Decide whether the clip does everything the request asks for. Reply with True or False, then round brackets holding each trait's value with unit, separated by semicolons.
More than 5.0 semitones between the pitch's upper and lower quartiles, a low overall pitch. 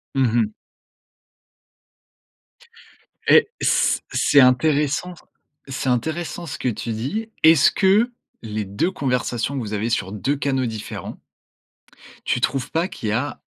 True (5.6 semitones; 130 Hz)